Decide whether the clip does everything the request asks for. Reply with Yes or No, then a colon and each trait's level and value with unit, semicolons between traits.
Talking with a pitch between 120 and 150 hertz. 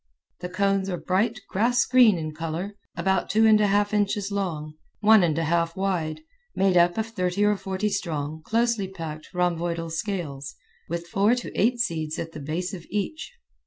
No: medium, 185 Hz